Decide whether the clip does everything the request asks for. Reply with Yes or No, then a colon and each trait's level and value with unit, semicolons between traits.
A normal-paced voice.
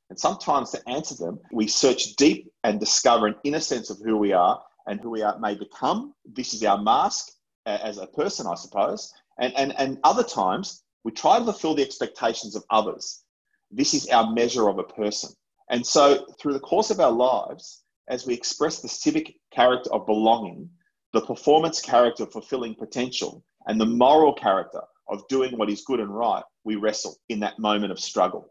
Yes: average, 195 wpm